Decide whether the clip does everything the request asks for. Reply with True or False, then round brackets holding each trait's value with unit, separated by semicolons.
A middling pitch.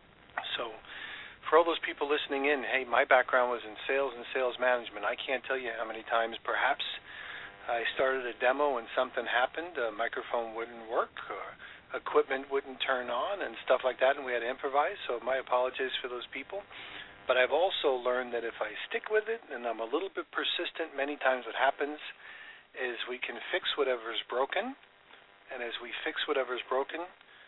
False (130 Hz)